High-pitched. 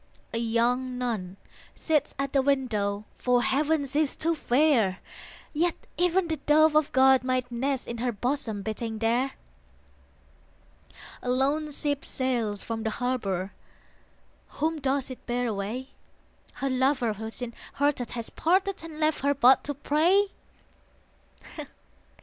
Yes: very high, 260 Hz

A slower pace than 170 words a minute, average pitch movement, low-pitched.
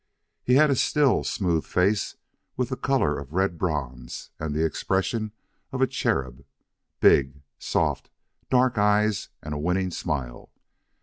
No: average, 140 wpm; wide, 8.0 semitones; very low, 95 Hz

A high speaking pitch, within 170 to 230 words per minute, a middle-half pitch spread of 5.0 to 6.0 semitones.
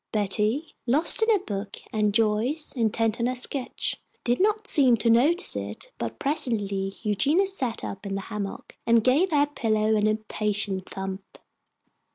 No: high, 225 Hz; average, 160 wpm; wide, 5.4 semitones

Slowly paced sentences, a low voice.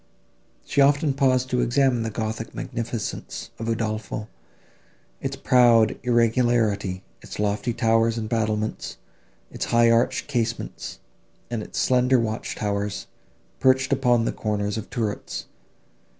Yes: slow, 120 wpm; low, 115 Hz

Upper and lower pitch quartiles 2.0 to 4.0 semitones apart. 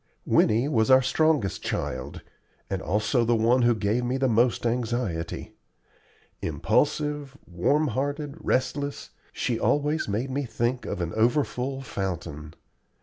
No: average, 4.4 semitones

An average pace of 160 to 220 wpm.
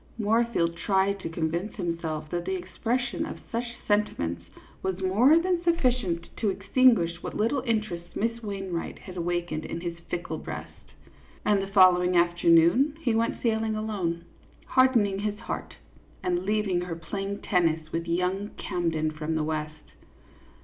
No: average, 150 wpm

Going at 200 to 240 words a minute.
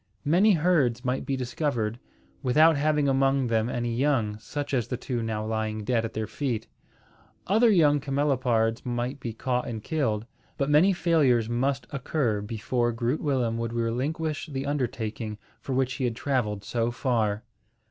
No: average, 160 wpm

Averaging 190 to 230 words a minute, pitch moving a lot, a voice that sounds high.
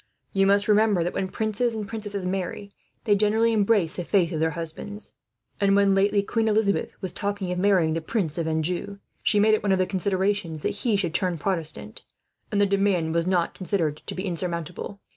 No: average, 200 wpm; average, 3.0 semitones; high, 195 Hz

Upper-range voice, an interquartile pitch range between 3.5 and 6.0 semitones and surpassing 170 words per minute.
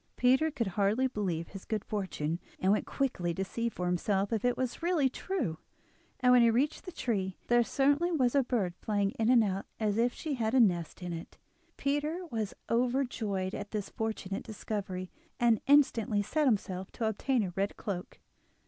Yes: high, 220 Hz; average, 4.8 semitones; average, 185 wpm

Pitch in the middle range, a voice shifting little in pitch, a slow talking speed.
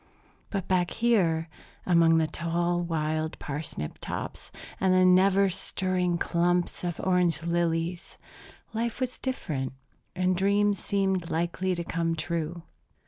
Yes: medium, 175 Hz; narrow, 2.2 semitones; slow, 125 wpm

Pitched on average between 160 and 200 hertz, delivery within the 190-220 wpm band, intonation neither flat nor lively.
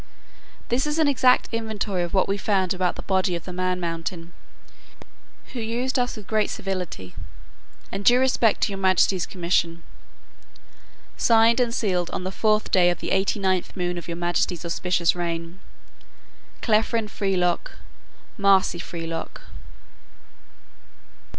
No: high, 190 Hz; average, 140 wpm; average, 3.7 semitones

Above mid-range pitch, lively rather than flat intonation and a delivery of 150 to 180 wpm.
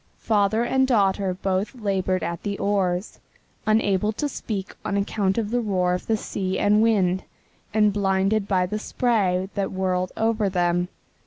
No: high, 200 Hz; narrow, 2.5 semitones; average, 160 wpm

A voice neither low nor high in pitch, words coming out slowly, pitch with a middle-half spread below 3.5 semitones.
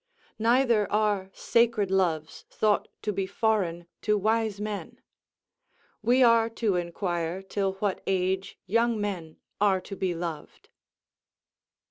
No: high, 200 Hz; slow, 120 wpm; average, 2.9 semitones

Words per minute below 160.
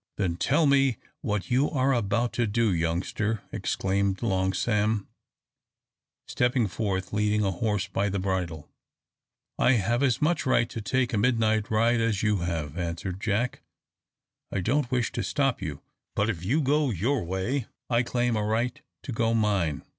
No: average, 165 wpm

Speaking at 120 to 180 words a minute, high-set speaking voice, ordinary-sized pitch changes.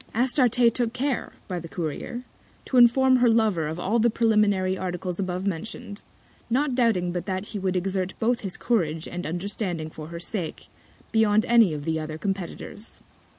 Yes: average, 165 wpm; high, 200 Hz; average, 4.8 semitones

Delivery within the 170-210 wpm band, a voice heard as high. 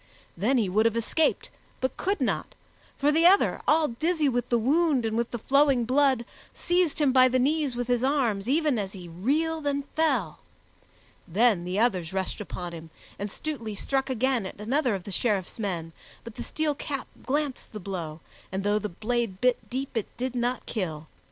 Yes: average, 190 wpm; high, 245 Hz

